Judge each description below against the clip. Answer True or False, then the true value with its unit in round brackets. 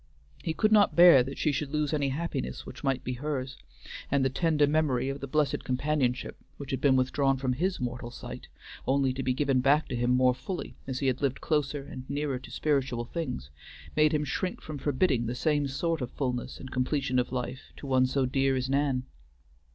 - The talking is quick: True (210 wpm)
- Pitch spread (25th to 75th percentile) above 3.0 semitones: False (2.6 semitones)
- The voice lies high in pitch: False (135 Hz)